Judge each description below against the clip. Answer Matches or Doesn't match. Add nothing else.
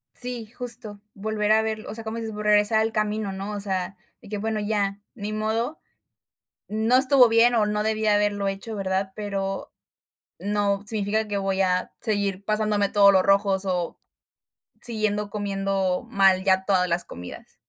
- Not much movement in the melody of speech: Matches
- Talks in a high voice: Matches